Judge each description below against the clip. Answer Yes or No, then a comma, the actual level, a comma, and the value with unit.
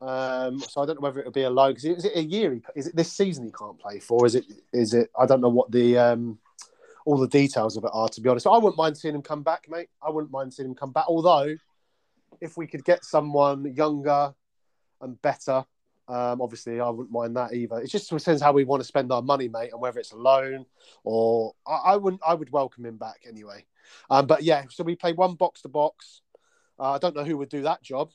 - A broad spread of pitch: No, average, 4.7 semitones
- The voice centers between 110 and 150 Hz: Yes, medium, 140 Hz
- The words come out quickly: Yes, fast, 255 wpm